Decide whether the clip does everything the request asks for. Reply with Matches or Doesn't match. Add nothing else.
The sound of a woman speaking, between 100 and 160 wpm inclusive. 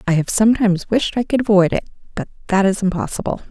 Doesn't match